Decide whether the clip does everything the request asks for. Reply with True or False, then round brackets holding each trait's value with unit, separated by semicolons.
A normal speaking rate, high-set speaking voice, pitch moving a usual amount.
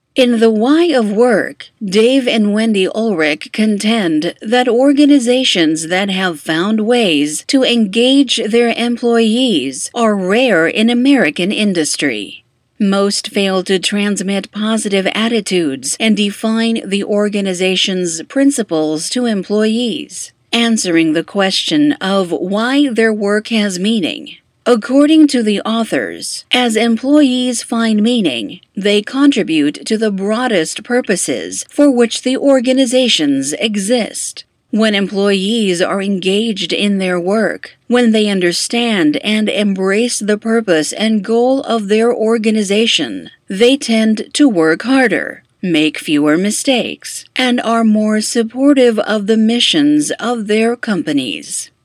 True (120 wpm; 220 Hz; 3.7 semitones)